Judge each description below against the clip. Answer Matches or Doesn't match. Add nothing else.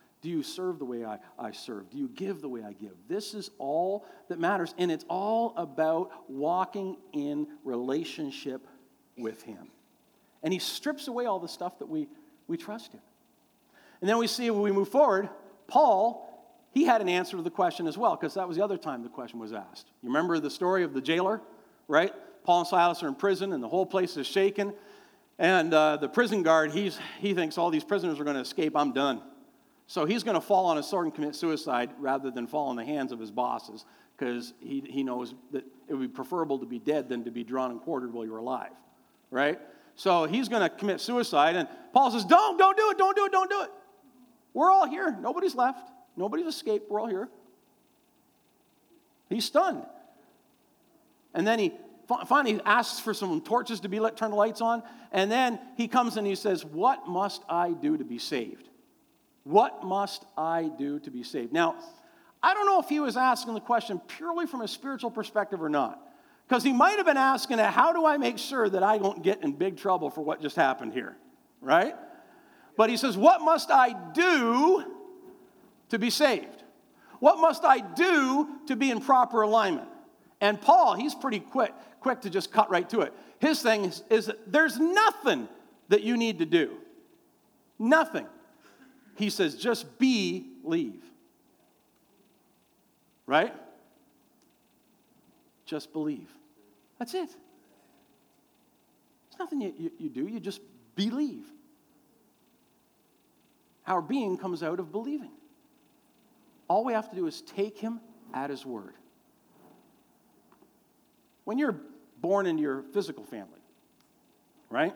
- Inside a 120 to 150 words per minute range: Doesn't match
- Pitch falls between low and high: Doesn't match